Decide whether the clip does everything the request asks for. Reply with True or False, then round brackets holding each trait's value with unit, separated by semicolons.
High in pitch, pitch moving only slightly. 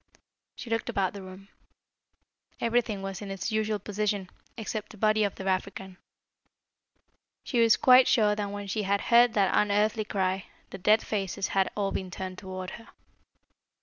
True (205 Hz; 2.1 semitones)